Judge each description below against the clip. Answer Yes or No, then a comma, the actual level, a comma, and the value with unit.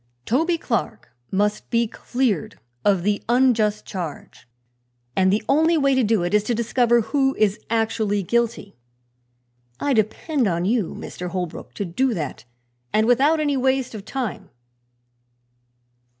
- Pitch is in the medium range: No, high, 225 Hz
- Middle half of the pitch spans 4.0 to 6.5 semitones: Yes, average, 4.4 semitones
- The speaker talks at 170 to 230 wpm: No, average, 140 wpm